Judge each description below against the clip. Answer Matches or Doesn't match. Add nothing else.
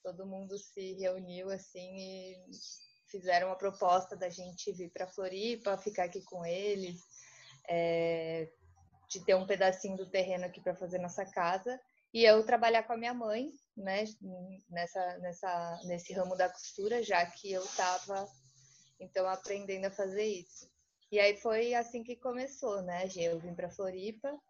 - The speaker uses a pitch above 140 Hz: Matches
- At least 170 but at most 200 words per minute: Doesn't match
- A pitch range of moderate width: Doesn't match